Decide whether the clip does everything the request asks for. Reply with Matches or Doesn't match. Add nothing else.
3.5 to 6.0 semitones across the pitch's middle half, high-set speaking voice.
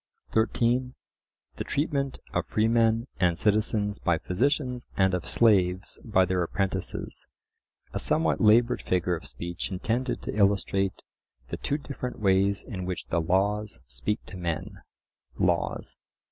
Doesn't match